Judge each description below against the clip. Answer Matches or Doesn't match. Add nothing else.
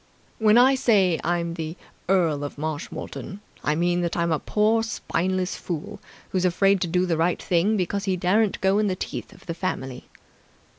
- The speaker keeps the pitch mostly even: Doesn't match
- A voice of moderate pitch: Matches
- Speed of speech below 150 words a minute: Doesn't match